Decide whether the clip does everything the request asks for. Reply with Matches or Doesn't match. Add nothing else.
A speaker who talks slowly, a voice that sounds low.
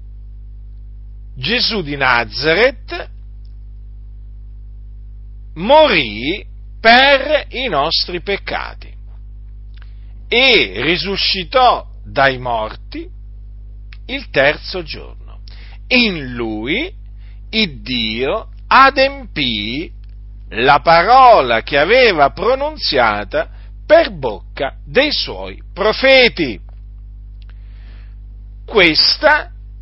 Matches